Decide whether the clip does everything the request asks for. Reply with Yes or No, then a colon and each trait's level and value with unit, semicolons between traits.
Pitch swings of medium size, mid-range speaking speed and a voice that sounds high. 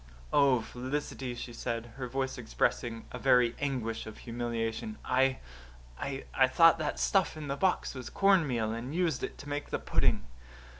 No: average, 3.6 semitones; average, 160 wpm; low, 130 Hz